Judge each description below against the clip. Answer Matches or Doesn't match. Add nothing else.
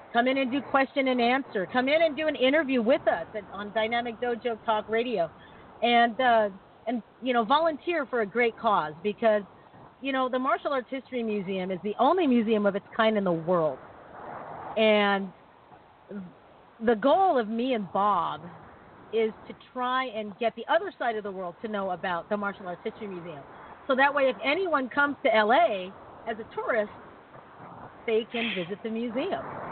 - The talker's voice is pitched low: Doesn't match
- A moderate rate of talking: Matches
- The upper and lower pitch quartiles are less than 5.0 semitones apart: Matches